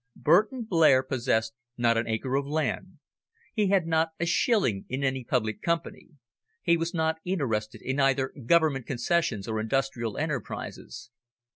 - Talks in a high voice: No, low, 135 Hz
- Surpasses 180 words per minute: No, average, 145 wpm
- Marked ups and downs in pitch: Yes, wide, 5.9 semitones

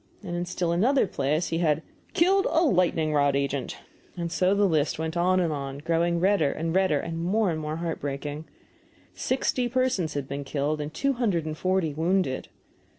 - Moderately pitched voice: Yes, medium, 165 Hz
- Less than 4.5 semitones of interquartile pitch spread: Yes, average, 3.8 semitones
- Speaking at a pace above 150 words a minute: Yes, average, 175 wpm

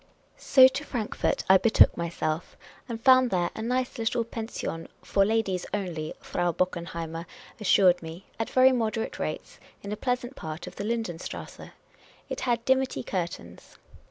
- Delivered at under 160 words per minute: No, average, 165 wpm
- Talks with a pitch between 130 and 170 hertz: No, high, 210 Hz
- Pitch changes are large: Yes, wide, 5.7 semitones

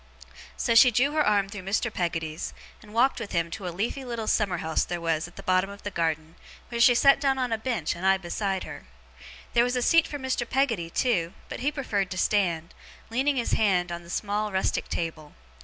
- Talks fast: Yes, fast, 225 wpm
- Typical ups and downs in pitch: No, wide, 5.9 semitones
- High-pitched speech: Yes, high, 205 Hz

